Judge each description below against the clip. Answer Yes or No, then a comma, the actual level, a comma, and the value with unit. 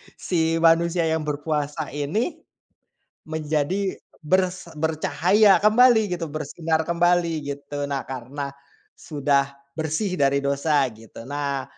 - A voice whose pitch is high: No, medium, 160 Hz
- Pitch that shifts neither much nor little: Yes, average, 3.5 semitones